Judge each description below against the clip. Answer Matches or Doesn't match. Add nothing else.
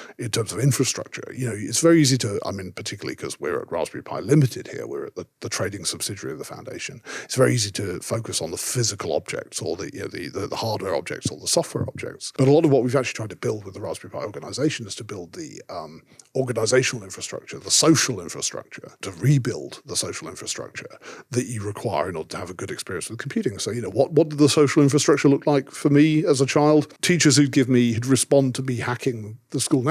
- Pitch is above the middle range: Doesn't match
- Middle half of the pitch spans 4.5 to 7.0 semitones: Doesn't match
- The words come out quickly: Matches